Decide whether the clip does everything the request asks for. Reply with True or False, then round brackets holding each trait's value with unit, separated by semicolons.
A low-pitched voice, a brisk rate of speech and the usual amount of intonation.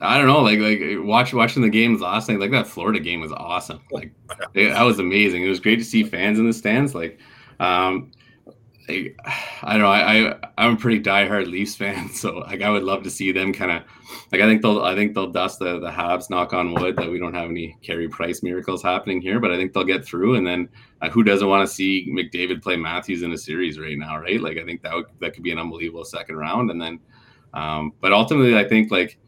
True (95 Hz; 250 wpm; 3.3 semitones)